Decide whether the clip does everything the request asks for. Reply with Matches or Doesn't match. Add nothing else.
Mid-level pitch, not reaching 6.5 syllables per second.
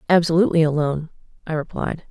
Doesn't match